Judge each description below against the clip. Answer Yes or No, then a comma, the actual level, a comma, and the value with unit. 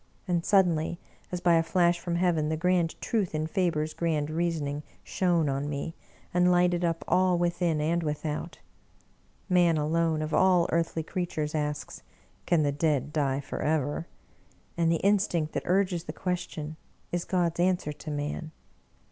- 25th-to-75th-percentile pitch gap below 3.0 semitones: Yes, narrow, 2.5 semitones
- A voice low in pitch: No, medium, 165 Hz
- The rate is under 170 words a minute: Yes, average, 160 wpm